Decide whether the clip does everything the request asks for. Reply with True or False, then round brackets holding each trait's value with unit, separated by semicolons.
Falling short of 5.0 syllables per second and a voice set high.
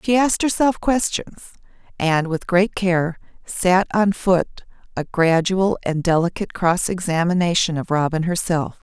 False (4.4 syllables/s; 180 Hz)